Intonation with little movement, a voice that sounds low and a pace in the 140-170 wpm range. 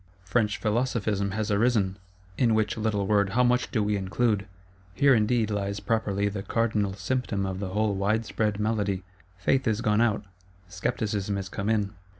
Yes: narrow, 2.1 semitones; low, 105 Hz; average, 165 wpm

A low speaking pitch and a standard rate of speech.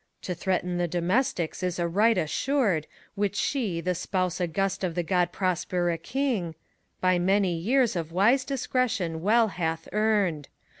No: medium, 185 Hz; average, 150 wpm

